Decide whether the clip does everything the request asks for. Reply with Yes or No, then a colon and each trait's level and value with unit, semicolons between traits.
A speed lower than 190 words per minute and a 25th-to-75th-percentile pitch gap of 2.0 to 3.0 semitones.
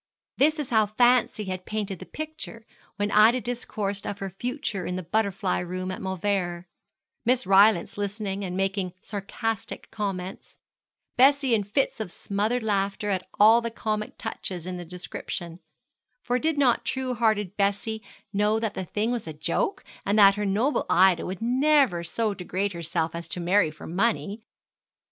No: average, 165 wpm; average, 3.6 semitones